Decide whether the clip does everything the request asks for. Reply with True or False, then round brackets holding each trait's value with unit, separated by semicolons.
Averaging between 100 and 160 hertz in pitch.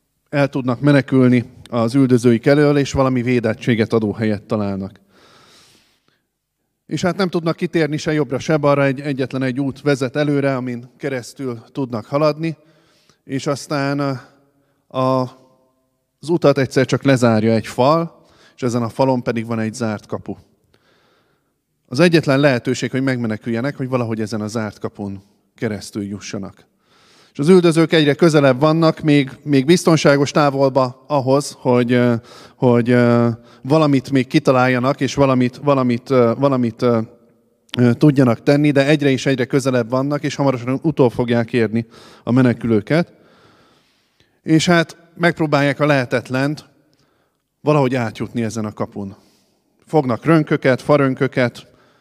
True (130 Hz)